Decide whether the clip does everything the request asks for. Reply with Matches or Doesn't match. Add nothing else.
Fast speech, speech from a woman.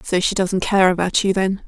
Matches